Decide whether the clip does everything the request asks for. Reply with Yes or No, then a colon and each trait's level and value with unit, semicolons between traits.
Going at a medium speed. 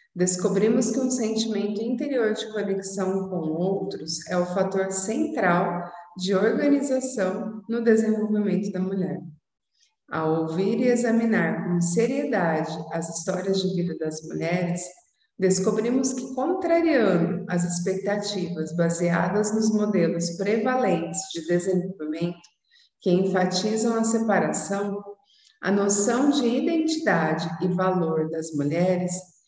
No: slow, 110 wpm